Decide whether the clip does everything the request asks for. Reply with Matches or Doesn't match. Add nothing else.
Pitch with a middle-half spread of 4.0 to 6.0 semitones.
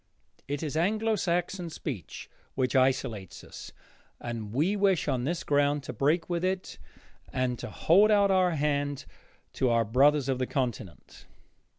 Matches